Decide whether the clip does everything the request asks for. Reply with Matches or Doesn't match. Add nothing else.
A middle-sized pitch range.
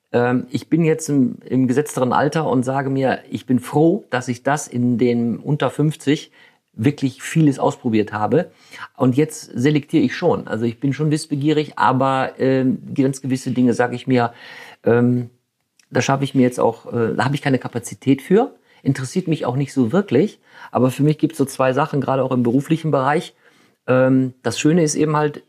Matches